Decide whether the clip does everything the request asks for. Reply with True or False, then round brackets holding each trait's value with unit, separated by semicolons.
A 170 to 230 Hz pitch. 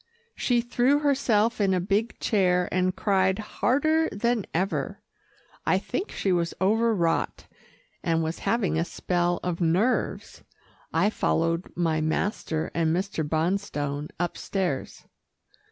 True (185 Hz)